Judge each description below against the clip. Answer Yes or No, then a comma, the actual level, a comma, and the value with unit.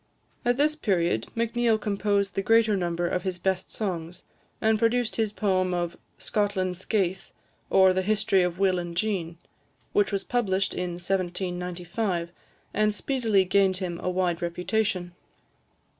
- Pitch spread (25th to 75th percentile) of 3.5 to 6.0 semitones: No, average, 3.1 semitones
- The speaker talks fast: No, average, 145 wpm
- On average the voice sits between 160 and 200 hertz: Yes, high, 190 Hz